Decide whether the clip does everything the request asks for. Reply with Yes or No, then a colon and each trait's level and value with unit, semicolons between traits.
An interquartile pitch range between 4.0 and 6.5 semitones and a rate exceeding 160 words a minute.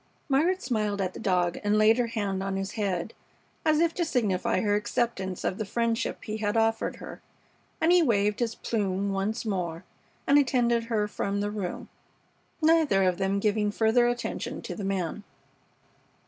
No: average, 3.4 semitones; average, 175 wpm